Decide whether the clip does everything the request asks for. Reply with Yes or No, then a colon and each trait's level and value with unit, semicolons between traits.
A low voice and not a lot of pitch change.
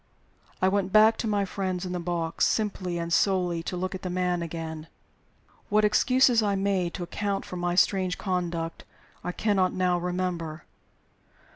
No: medium, 185 Hz; narrow, 2.2 semitones